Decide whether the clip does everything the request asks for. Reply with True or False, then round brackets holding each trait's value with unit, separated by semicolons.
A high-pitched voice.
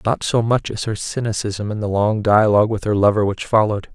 False (105 Hz)